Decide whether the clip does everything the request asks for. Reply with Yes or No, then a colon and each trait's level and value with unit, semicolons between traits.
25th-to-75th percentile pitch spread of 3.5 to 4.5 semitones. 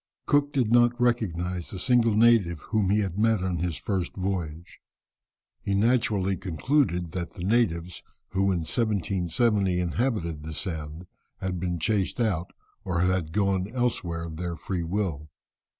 Yes: average, 4.2 semitones